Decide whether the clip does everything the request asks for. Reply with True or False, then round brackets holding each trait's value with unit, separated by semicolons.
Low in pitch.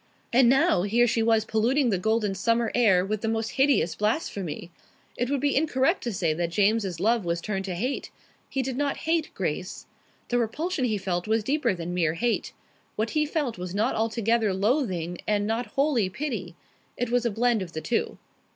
False (225 Hz)